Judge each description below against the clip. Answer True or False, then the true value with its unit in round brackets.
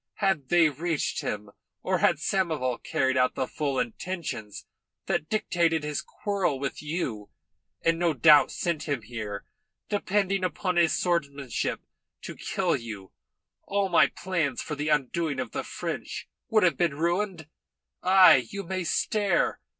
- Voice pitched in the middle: True (160 Hz)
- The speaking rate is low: False (145 wpm)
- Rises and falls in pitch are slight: False (5.2 semitones)